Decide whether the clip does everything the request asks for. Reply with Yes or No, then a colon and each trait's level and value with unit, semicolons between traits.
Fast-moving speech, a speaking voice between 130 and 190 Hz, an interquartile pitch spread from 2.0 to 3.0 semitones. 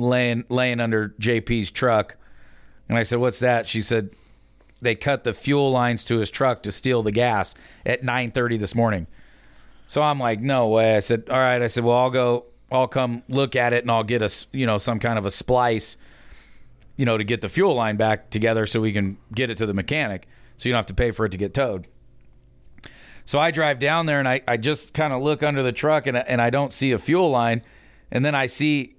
No: fast, 235 wpm; low, 120 Hz; average, 2.7 semitones